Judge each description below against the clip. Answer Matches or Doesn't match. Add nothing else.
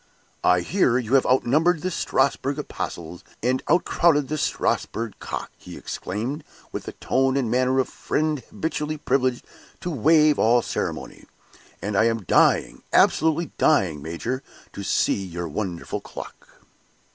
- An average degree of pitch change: Doesn't match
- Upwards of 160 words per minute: Doesn't match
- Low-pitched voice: Matches